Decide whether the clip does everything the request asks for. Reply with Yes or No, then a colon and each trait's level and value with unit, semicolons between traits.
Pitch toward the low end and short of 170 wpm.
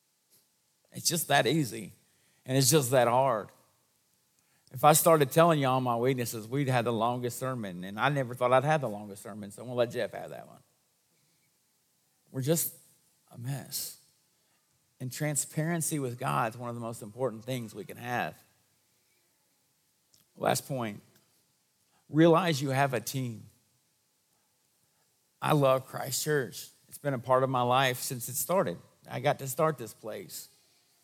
Yes: low, 130 Hz; average, 160 wpm